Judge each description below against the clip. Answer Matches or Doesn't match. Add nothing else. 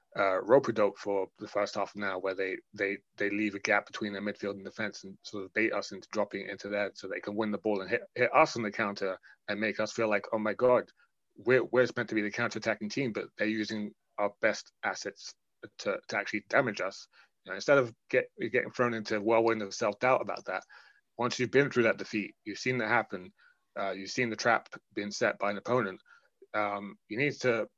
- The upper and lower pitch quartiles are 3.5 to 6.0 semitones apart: Doesn't match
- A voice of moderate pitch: Doesn't match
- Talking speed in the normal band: Doesn't match